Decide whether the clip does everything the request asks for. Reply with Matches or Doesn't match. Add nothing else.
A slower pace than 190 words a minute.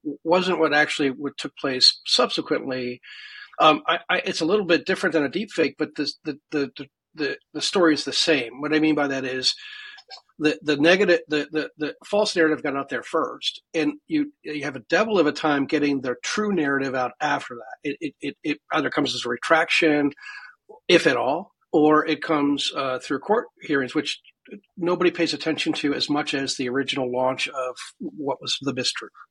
Doesn't match